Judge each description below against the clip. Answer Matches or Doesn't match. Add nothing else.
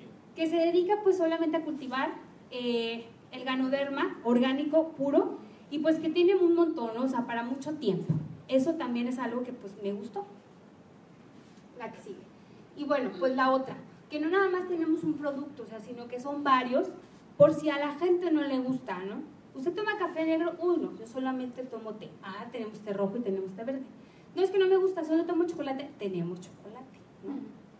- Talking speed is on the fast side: Matches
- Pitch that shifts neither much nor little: Doesn't match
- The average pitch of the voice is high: Matches